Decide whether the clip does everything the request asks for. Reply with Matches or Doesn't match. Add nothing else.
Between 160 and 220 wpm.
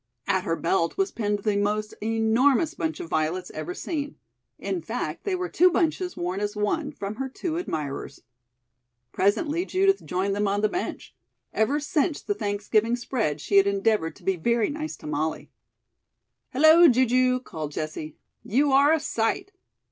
Matches